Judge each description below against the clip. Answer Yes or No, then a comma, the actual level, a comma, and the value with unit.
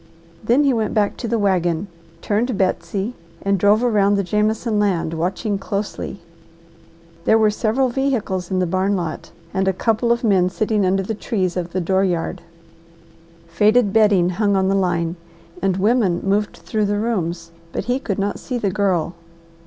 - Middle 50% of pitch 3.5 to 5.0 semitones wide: No, average, 2.8 semitones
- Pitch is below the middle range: No, high, 200 Hz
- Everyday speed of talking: Yes, average, 175 wpm